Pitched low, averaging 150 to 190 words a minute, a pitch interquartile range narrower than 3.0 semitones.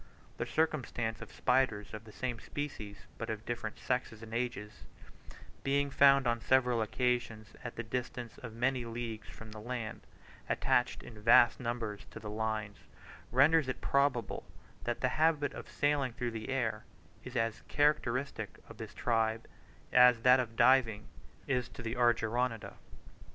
Yes: low, 120 Hz; average, 155 wpm; narrow, 2.5 semitones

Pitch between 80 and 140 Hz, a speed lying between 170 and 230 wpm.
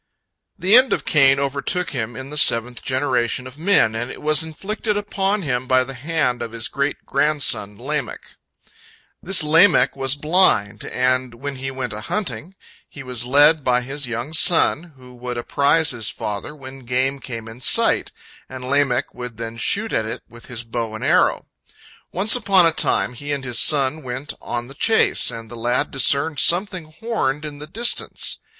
Yes: low, 135 Hz; average, 180 wpm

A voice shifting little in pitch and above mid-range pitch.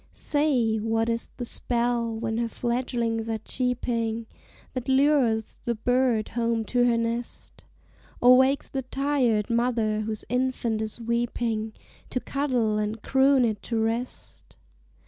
Yes: narrow, 2.0 semitones; high, 235 Hz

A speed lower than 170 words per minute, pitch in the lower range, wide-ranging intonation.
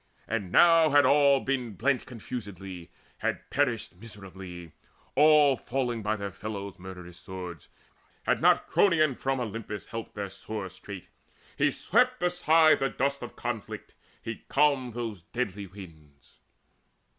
Yes: average, 140 wpm; low, 115 Hz; wide, 6.4 semitones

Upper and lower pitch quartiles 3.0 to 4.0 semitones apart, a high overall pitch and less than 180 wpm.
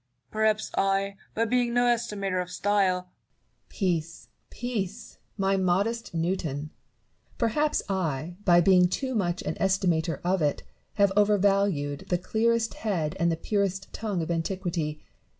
Yes: average, 3.6 semitones; high, 195 Hz; slow, 135 wpm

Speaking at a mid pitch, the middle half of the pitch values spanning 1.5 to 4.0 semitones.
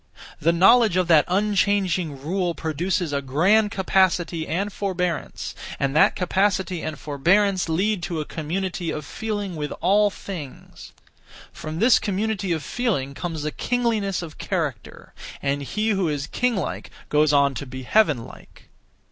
No: medium, 180 Hz; average, 4.7 semitones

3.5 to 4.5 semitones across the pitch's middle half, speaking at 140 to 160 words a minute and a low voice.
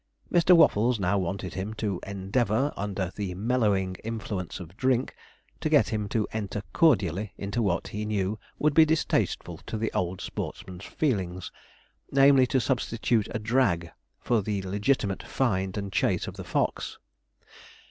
Yes: average, 4.1 semitones; average, 150 wpm; low, 105 Hz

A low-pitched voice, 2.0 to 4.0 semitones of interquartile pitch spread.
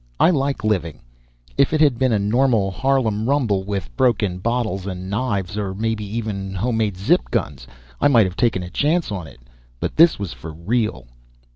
No: low, 105 Hz; average, 4.6 semitones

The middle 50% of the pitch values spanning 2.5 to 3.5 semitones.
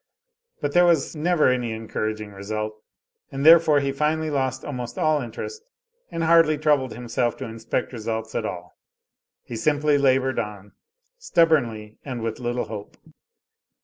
No: average, 5.3 semitones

